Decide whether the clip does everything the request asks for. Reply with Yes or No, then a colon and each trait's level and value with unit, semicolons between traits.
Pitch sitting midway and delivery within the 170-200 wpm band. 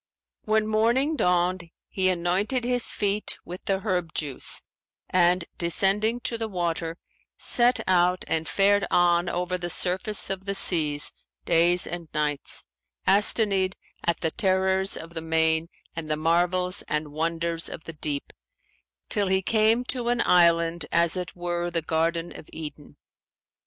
No: medium, 180 Hz; average, 145 wpm